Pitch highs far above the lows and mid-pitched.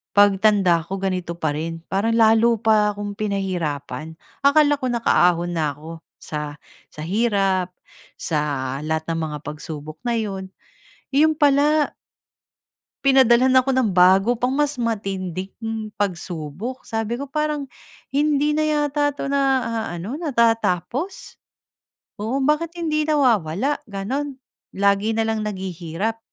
No: wide, 7.0 semitones; high, 220 Hz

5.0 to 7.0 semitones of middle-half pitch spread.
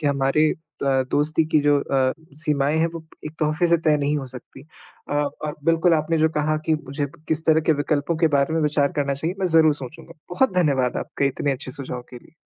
No: narrow, 2.4 semitones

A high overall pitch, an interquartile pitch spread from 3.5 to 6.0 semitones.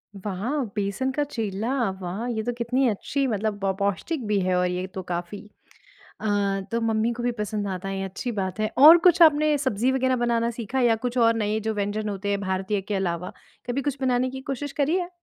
Yes: high, 220 Hz; average, 4.5 semitones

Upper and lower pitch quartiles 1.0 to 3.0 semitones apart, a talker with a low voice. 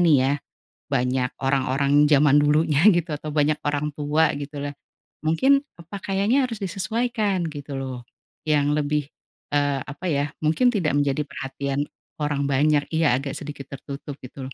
No: narrow, 2.5 semitones; medium, 145 Hz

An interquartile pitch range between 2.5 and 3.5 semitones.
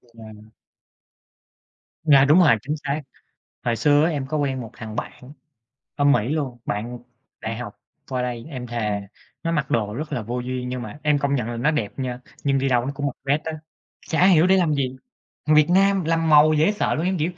No: average, 4.2 semitones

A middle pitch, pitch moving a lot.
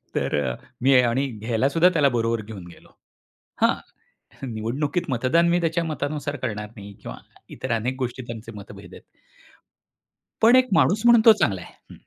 No: low, 130 Hz; wide, 6.5 semitones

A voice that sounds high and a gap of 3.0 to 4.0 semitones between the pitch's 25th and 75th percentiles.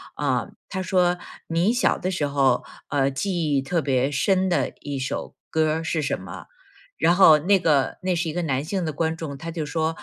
No: medium, 160 Hz; average, 3.7 semitones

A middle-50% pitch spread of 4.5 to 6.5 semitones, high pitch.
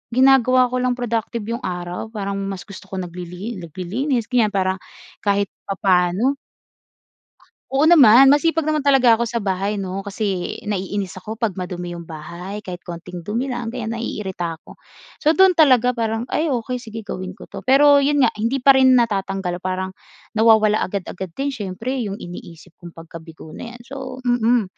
Yes: average, 5.2 semitones; high, 215 Hz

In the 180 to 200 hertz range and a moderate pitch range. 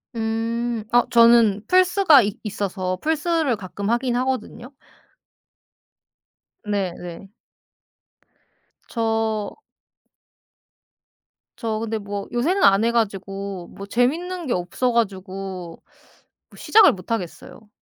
No: high, 225 Hz; average, 3.8 semitones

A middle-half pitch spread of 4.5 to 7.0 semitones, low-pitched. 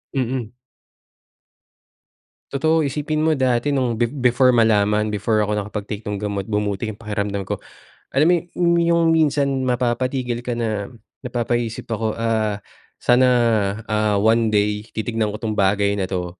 No: average, 3.5 semitones; low, 115 Hz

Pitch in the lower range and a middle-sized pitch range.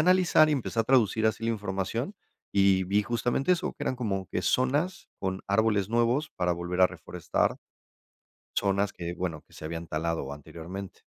Yes: low, 100 Hz; average, 4.9 semitones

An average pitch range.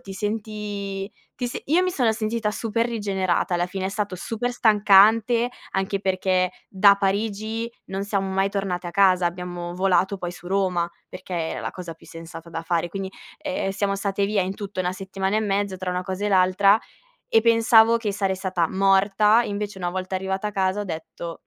No: narrow, 2.2 semitones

